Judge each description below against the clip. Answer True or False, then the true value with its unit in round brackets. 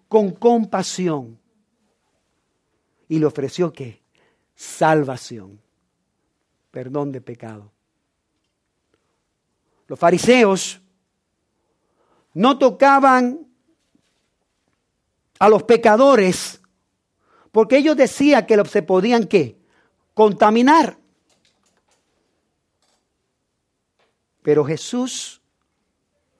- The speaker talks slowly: True (60 wpm)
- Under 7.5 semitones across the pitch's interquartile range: False (8.1 semitones)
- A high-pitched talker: True (200 Hz)